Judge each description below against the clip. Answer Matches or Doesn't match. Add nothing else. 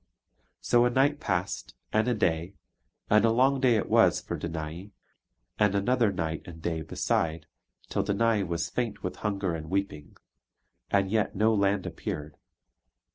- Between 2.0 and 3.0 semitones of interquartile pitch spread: Doesn't match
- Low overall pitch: Matches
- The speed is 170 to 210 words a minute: Doesn't match